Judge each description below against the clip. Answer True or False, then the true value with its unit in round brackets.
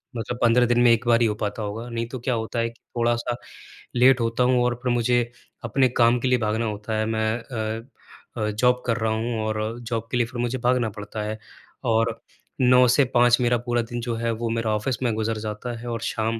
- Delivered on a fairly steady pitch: True (1.6 semitones)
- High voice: False (115 Hz)